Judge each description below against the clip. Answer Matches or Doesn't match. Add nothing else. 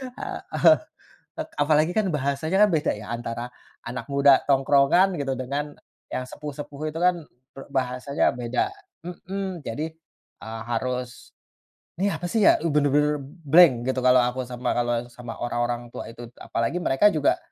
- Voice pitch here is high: Doesn't match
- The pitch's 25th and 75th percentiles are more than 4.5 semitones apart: Doesn't match